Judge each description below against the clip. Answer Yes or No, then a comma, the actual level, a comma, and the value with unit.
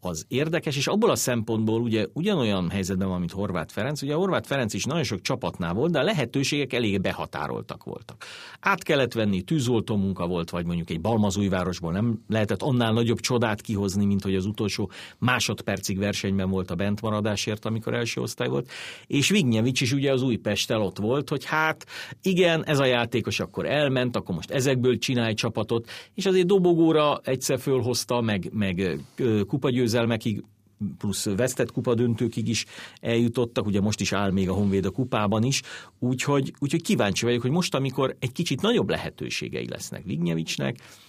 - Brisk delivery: Yes, fast, 170 wpm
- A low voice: Yes, low, 115 Hz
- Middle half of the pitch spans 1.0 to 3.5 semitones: No, average, 4.7 semitones